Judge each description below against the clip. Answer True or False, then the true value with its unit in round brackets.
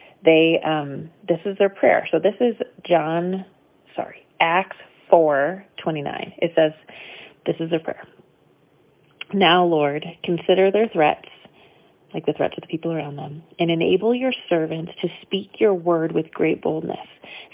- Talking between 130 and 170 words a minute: True (155 wpm)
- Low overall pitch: False (170 Hz)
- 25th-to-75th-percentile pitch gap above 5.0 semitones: False (3.1 semitones)